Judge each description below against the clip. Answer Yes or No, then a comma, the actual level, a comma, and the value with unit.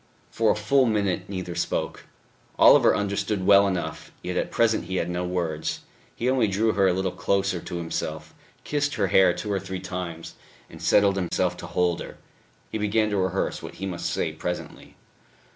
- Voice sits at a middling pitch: No, very low, 95 Hz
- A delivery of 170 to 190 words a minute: Yes, average, 185 wpm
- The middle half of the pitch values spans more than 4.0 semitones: No, average, 2.7 semitones